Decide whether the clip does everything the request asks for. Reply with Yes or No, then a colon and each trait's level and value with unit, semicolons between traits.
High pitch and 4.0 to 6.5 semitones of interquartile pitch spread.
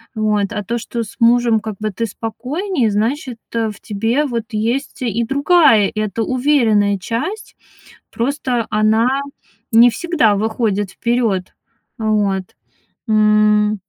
No: high, 225 Hz; narrow, 2.5 semitones